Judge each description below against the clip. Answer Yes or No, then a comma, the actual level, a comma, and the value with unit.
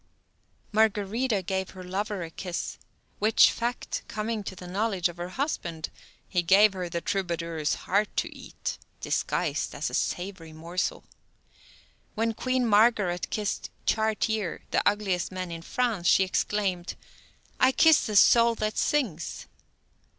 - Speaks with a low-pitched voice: No, high, 195 Hz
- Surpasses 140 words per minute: No, slow, 135 wpm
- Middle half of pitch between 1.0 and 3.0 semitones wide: No, average, 3.7 semitones